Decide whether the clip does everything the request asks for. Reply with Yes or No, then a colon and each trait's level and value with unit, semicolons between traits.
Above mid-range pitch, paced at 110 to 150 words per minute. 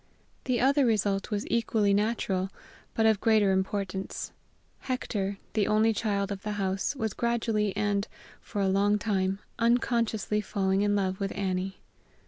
Yes: high, 205 Hz; average, 145 wpm